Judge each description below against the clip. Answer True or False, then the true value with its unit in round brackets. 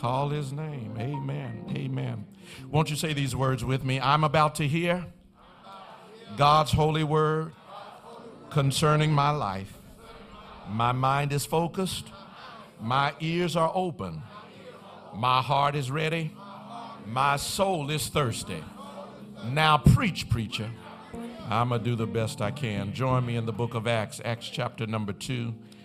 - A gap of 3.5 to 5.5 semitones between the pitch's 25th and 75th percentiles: True (4.8 semitones)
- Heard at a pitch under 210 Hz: True (140 Hz)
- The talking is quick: False (140 wpm)